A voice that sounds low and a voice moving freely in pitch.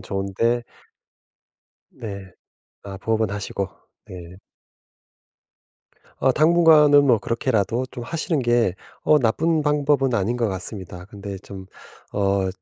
Yes: low, 115 Hz; wide, 6.0 semitones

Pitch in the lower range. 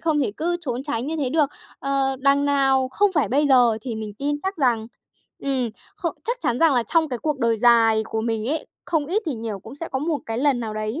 No: very high, 270 Hz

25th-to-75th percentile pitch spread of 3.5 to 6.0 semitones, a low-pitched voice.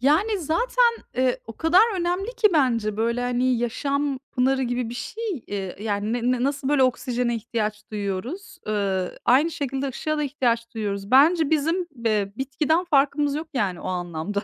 No: wide, 5.5 semitones; very high, 255 Hz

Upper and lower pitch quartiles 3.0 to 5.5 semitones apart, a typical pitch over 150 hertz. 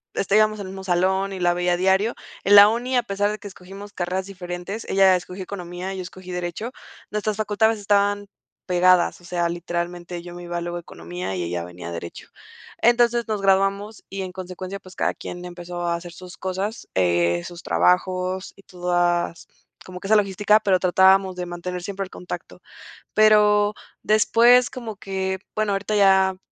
No: narrow, 2.4 semitones; high, 190 Hz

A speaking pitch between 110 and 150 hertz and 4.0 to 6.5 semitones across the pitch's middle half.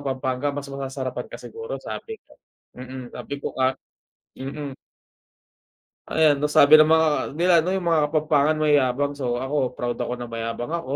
No: medium, 140 Hz; average, 2.9 semitones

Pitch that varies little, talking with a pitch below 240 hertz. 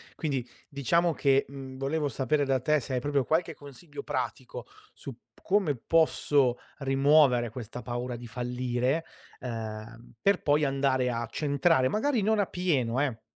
No: average, 3.5 semitones; low, 135 Hz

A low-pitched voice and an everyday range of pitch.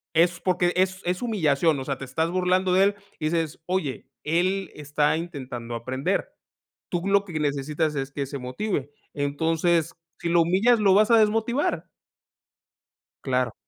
No: medium, 165 Hz; average, 4.7 semitones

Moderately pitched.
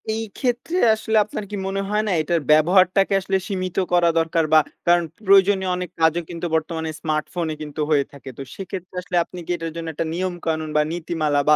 Yes: medium, 175 Hz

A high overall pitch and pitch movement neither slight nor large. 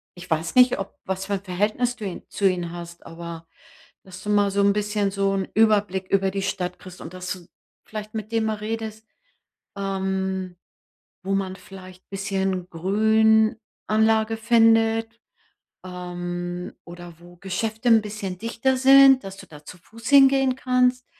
Yes: high, 195 Hz; average, 3.3 semitones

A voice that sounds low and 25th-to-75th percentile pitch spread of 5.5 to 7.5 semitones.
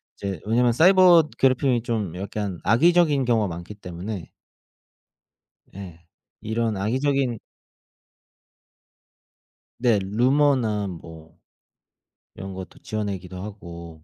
No: low, 105 Hz; average, 5.1 semitones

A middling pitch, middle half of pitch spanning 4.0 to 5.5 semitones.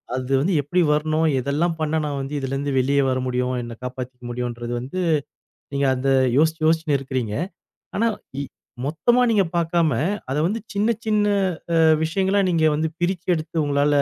Yes: medium, 150 Hz; average, 4.7 semitones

